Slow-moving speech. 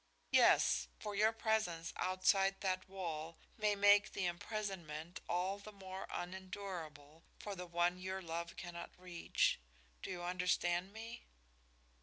Yes: slow, 130 wpm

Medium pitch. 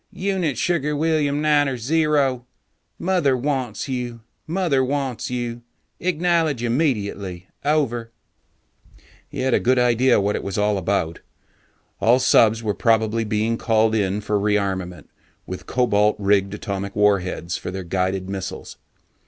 No: low, 115 Hz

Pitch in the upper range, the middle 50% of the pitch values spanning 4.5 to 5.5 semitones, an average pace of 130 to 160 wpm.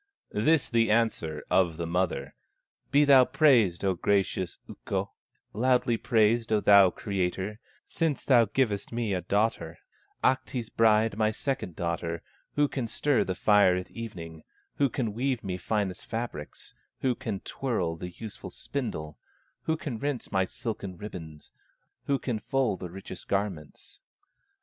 No: low, 105 Hz; average, 5.1 semitones; average, 145 wpm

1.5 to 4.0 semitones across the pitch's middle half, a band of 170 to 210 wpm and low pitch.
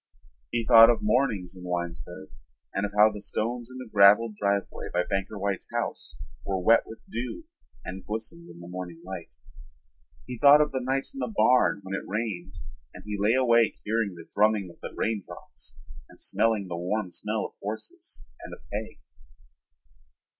Yes: average, 3.5 semitones; average, 175 wpm; low, 105 Hz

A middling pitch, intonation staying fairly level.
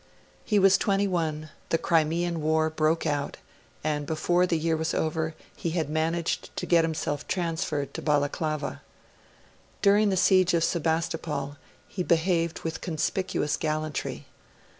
Yes: medium, 160 Hz; narrow, 2.0 semitones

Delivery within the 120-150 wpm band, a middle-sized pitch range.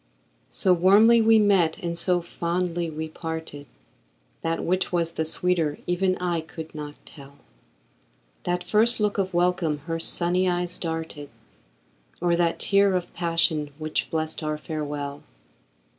No: average, 140 wpm; narrow, 2.2 semitones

